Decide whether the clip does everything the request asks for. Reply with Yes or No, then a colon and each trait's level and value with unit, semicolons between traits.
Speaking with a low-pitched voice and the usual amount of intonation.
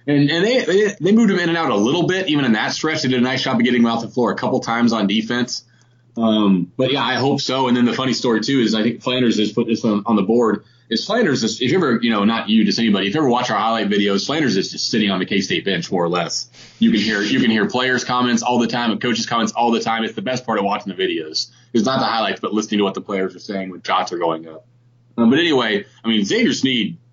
Yes: low, 120 Hz; average, 3.0 semitones